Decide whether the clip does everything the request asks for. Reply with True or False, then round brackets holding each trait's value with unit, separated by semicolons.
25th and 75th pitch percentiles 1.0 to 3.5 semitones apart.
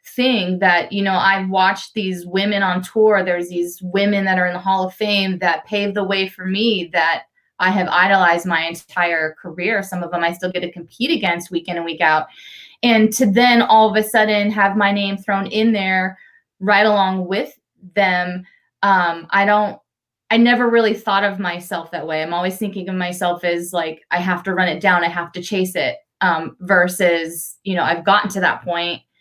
True (2.6 semitones)